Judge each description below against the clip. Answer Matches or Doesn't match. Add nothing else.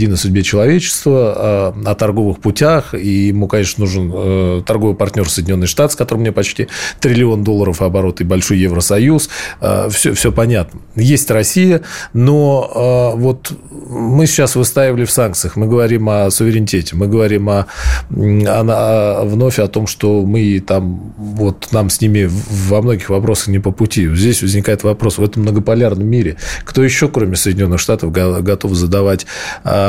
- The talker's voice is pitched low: Matches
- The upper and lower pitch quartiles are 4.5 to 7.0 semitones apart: Doesn't match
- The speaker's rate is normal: Matches